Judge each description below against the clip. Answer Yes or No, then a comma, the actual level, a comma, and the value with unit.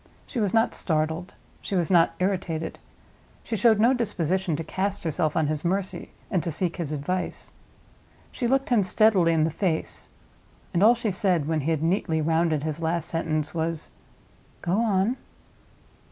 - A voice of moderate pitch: Yes, medium, 175 Hz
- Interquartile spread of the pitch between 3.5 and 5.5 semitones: Yes, average, 3.8 semitones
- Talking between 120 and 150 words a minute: No, average, 165 wpm